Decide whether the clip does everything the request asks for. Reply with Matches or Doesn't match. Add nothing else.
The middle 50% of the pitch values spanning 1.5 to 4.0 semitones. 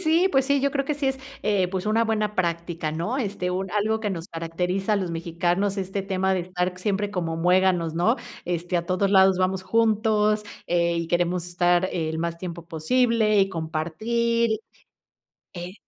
Matches